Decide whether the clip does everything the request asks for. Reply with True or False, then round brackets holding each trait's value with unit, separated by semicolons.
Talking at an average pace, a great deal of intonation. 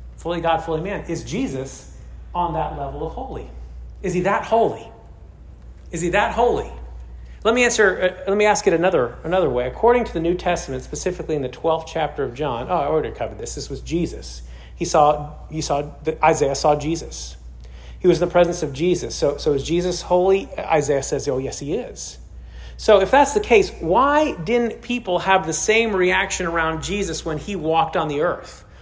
True (195 wpm; 7.0 semitones)